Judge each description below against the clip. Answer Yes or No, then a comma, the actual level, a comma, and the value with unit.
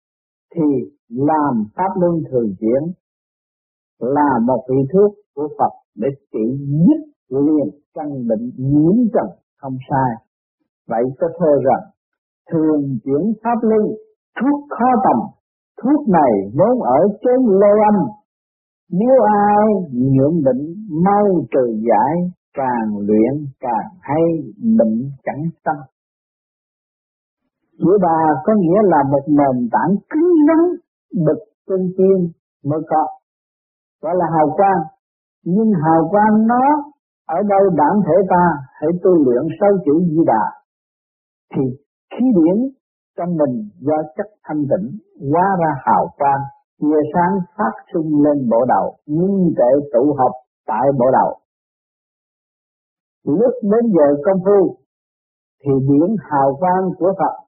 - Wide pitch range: Yes, wide, 6.5 semitones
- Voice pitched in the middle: Yes, medium, 165 Hz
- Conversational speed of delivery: No, slow, 135 wpm